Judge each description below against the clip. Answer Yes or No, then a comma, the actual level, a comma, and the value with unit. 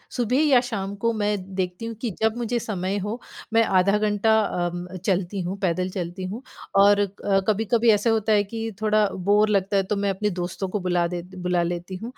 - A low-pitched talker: No, high, 205 Hz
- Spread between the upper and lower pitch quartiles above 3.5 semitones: No, average, 3.0 semitones